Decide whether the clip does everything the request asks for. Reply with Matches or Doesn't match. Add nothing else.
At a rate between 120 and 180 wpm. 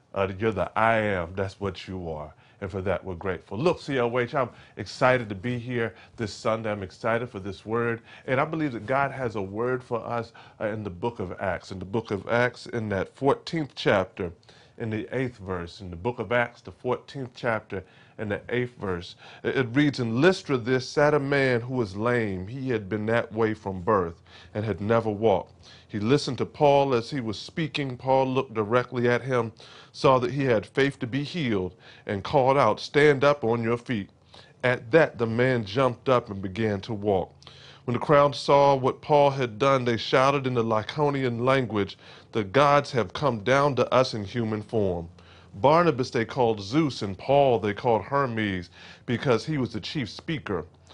Doesn't match